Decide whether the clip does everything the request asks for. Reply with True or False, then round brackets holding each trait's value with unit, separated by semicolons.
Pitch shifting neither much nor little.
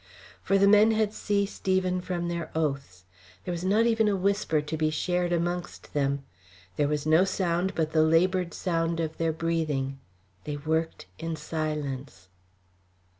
True (3.3 semitones)